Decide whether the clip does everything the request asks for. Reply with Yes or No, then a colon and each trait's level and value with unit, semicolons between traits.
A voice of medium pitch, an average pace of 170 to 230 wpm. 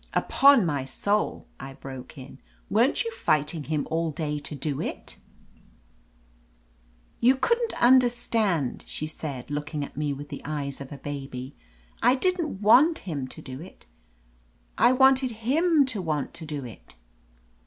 No: medium, 155 Hz; average, 160 wpm